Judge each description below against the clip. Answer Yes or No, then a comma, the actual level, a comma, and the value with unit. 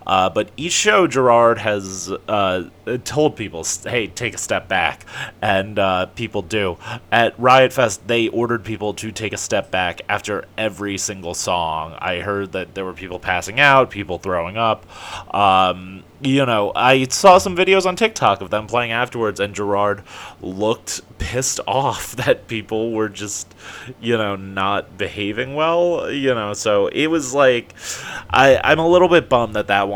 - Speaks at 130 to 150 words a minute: No, average, 170 wpm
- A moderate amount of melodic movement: Yes, average, 4.7 semitones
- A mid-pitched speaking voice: No, low, 110 Hz